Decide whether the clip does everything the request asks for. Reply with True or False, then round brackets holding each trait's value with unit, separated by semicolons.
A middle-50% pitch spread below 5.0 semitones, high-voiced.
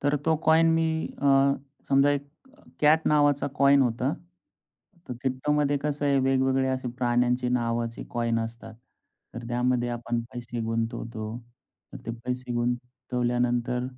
False (2.7 semitones; 125 Hz)